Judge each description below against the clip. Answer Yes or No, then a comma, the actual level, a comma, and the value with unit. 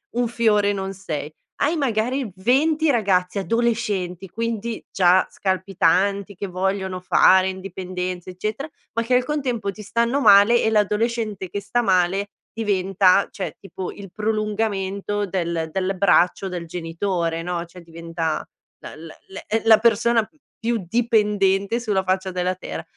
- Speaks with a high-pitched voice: Yes, high, 200 Hz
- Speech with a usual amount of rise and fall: Yes, average, 3.4 semitones